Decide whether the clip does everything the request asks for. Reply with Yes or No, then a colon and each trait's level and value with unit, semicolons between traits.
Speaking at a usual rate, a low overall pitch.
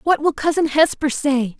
No: average, 190 wpm; very high, 290 Hz